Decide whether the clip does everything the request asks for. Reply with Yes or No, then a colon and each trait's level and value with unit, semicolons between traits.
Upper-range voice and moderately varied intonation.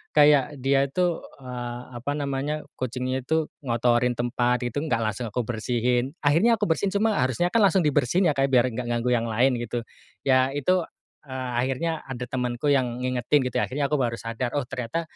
No: low, 130 Hz; average, 3.3 semitones